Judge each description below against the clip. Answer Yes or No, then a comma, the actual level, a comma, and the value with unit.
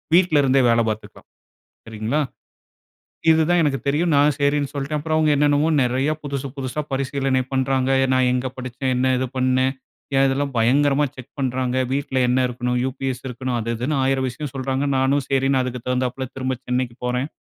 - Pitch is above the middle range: No, low, 130 Hz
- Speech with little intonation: Yes, narrow, 1.9 semitones